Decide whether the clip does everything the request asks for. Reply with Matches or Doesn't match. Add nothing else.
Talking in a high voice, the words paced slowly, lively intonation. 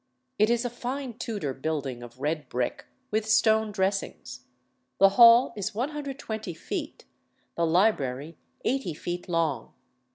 Matches